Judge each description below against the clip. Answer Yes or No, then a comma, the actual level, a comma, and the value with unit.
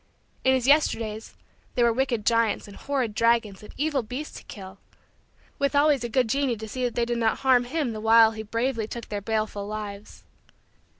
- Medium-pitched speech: No, high, 230 Hz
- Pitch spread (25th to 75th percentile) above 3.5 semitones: No, average, 3.2 semitones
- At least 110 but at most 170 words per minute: No, average, 195 wpm